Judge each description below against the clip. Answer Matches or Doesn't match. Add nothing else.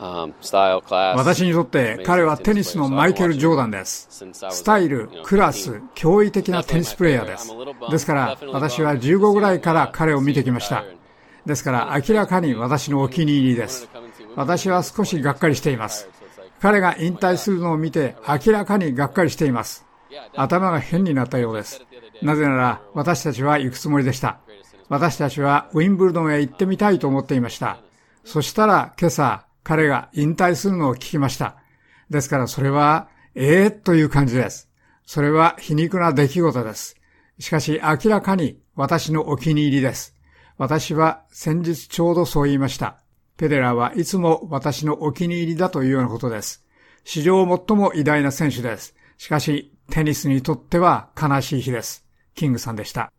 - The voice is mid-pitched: Matches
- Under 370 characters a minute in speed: Matches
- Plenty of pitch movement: Doesn't match